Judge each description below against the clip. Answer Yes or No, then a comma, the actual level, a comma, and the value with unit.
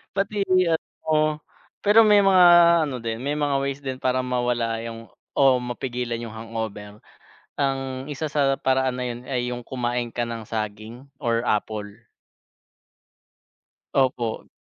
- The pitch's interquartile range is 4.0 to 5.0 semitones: No, average, 3.3 semitones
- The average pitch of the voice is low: Yes, low, 125 Hz